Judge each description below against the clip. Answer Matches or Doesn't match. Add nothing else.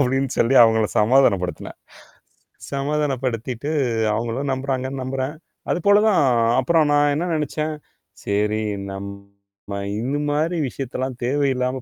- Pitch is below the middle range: Matches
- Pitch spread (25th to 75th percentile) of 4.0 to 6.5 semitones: Matches